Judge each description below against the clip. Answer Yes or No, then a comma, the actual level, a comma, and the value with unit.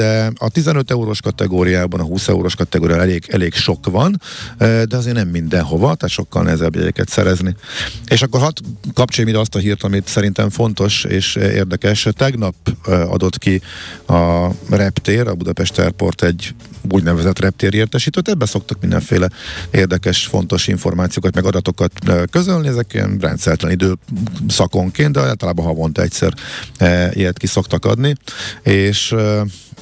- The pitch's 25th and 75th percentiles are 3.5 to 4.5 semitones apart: Yes, average, 3.8 semitones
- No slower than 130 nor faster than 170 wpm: Yes, average, 140 wpm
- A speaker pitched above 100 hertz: No, very low, 95 Hz